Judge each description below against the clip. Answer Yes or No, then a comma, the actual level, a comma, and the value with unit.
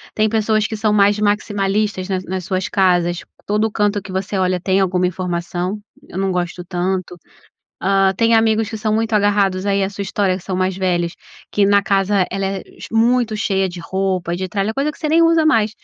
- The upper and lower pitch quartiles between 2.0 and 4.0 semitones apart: Yes, narrow, 2.4 semitones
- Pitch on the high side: Yes, high, 195 Hz